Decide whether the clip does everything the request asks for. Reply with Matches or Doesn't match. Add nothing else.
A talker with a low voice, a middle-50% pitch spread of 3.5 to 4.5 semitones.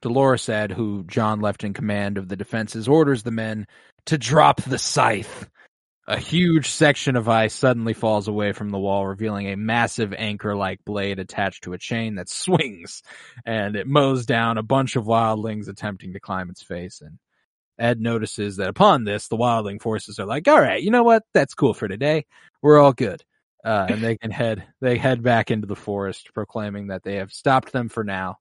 Matches